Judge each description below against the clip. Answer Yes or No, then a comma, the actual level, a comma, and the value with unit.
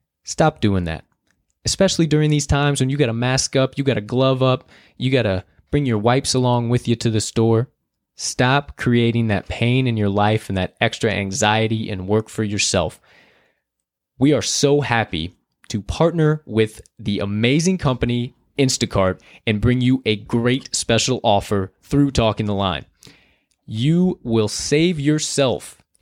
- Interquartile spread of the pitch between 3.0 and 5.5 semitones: Yes, average, 4.1 semitones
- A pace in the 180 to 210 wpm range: No, average, 165 wpm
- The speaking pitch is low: Yes, low, 115 Hz